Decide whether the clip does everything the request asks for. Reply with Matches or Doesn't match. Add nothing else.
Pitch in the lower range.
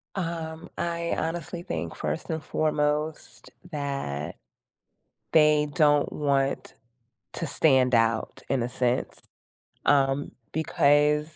Doesn't match